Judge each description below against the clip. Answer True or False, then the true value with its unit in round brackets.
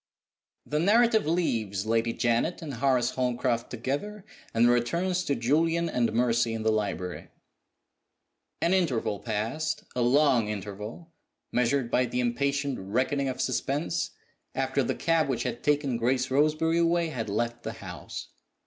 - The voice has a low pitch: True (130 Hz)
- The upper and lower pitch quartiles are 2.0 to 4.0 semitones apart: False (4.9 semitones)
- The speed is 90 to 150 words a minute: True (140 wpm)